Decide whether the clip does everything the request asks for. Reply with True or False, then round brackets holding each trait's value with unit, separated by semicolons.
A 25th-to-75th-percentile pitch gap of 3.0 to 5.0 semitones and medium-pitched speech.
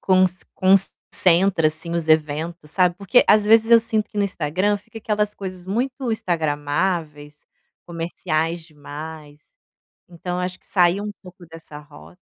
True (3.9 semitones; 175 Hz)